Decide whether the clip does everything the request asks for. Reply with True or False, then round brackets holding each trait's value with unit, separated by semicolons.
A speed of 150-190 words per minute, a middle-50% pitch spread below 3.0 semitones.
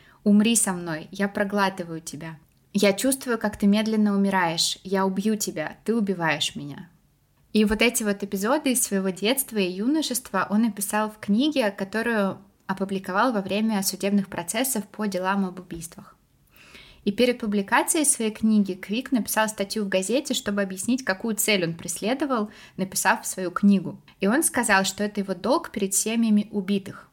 True (155 wpm; 2.6 semitones)